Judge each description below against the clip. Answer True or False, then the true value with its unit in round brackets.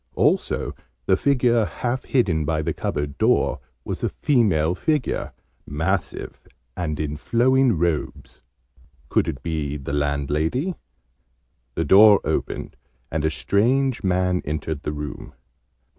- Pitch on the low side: True (85 Hz)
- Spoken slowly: True (125 wpm)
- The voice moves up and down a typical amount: False (7.8 semitones)